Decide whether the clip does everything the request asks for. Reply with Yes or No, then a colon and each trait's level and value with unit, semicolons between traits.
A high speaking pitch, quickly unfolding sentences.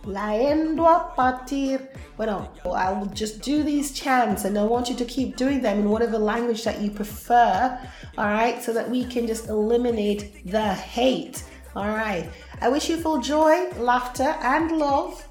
No: high, 240 Hz; average, 160 wpm